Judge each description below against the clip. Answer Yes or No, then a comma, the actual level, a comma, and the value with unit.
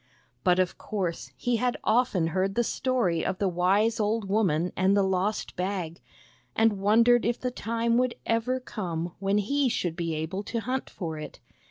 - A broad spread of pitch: No, average, 4.3 semitones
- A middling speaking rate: Yes, average, 180 wpm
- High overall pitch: Yes, high, 205 Hz